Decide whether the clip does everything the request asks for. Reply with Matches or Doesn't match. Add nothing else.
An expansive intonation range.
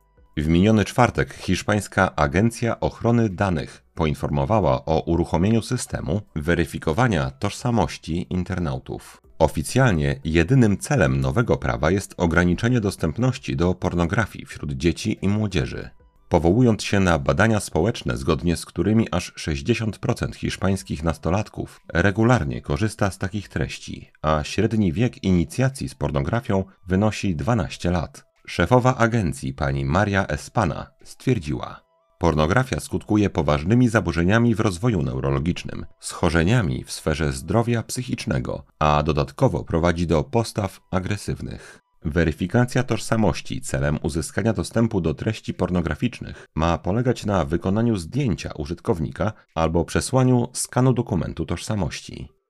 Matches